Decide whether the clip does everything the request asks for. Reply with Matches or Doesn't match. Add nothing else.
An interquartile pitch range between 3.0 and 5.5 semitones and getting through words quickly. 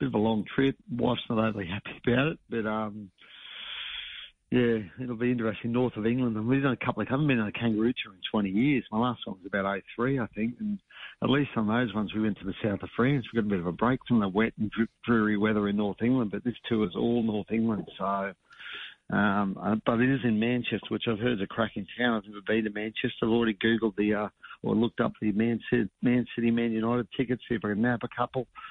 Doesn't match